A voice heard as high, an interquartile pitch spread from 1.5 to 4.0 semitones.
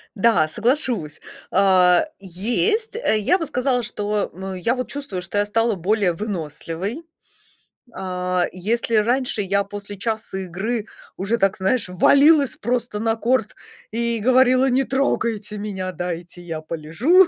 No: high, 210 Hz; average, 4.8 semitones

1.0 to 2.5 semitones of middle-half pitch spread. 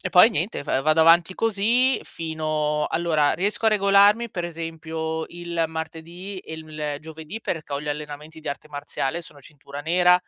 No: average, 2.9 semitones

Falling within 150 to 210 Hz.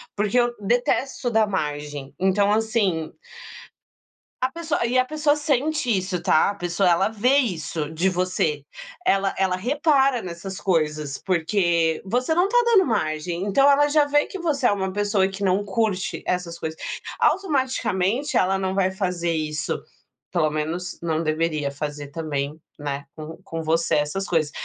Yes: high, 190 Hz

